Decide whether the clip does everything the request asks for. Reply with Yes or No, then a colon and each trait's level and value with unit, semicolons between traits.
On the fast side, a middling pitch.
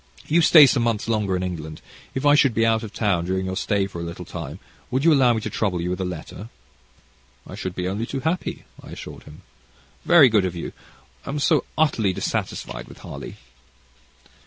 No: fast, 210 wpm; low, 105 Hz